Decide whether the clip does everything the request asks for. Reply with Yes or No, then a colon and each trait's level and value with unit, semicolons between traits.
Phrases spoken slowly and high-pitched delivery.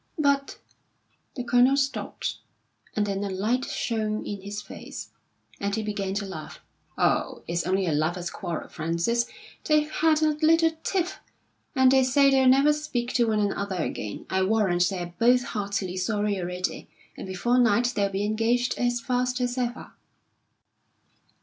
No: average, 160 wpm; high, 220 Hz